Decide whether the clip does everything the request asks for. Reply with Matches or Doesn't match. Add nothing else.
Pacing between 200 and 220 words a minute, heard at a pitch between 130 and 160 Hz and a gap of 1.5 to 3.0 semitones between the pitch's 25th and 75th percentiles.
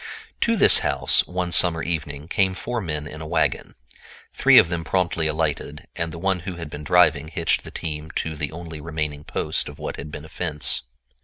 Doesn't match